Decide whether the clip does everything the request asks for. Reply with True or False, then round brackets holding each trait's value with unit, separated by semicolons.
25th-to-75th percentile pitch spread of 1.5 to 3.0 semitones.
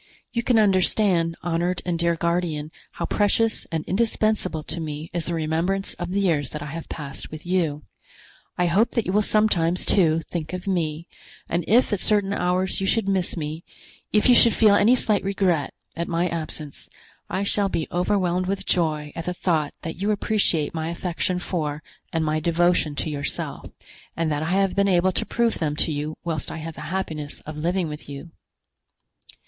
False (3.6 semitones)